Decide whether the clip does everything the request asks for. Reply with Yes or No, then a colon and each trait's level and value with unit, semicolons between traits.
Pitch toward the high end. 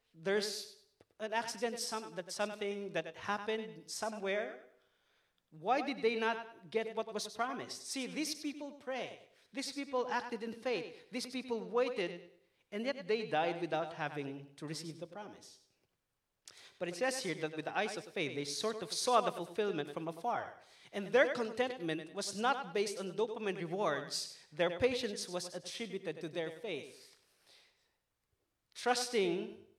Yes: high, 210 Hz